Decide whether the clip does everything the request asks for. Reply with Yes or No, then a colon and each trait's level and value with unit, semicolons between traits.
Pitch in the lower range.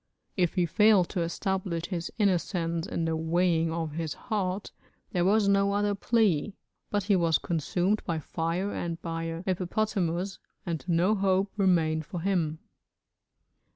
No: medium, 180 Hz